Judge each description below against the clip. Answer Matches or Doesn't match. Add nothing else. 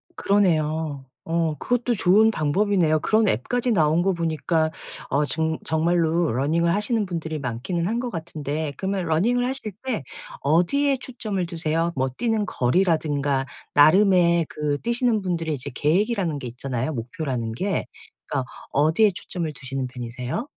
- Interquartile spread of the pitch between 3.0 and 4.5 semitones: Doesn't match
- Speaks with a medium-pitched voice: Matches